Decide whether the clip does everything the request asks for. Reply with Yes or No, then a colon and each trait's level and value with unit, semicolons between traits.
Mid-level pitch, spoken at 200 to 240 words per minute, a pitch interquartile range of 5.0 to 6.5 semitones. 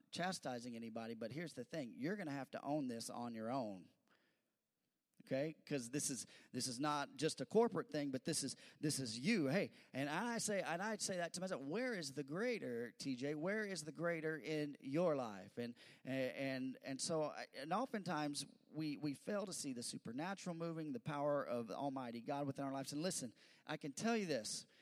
Yes: medium, 150 Hz; fast, 205 wpm; wide, 5.4 semitones